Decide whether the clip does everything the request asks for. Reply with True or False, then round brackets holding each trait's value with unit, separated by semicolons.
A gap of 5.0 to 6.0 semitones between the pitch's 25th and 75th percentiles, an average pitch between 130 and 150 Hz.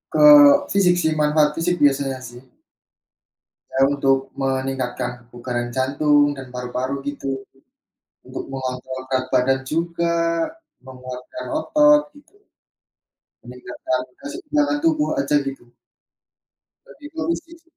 True (5.5 semitones; 135 Hz)